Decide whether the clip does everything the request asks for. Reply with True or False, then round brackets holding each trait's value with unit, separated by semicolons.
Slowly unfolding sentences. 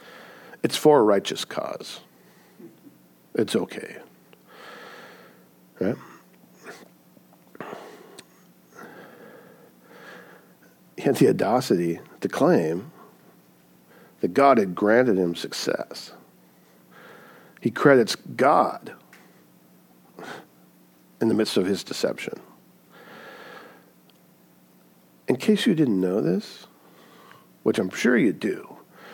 True (80 wpm)